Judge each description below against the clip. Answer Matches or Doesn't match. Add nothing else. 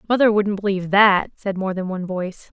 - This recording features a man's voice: Doesn't match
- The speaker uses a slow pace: Doesn't match